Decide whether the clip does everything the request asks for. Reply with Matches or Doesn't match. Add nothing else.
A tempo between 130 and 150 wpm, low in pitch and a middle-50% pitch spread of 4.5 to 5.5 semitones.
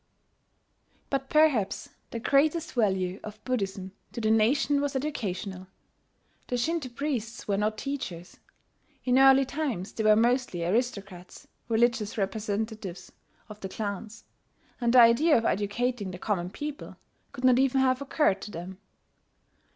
Doesn't match